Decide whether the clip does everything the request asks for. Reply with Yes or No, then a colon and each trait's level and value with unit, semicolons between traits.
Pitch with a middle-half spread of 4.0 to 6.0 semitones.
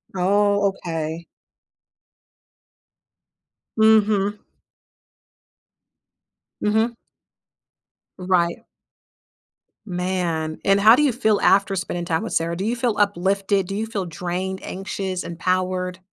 No: narrow, 2.6 semitones